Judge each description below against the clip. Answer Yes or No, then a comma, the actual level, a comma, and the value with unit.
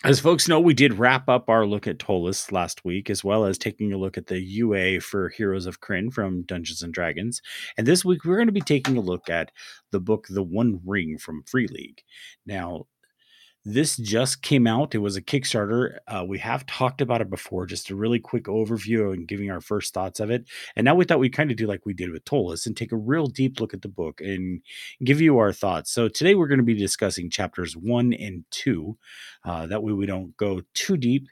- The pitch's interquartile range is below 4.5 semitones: No, average, 5.2 semitones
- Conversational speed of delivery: No, fast, 235 wpm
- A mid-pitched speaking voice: No, low, 110 Hz